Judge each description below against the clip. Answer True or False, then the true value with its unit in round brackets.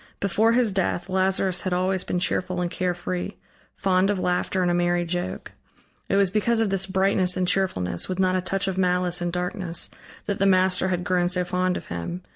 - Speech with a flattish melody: True (1.3 semitones)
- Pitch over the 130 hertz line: True (185 Hz)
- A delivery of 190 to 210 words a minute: True (205 wpm)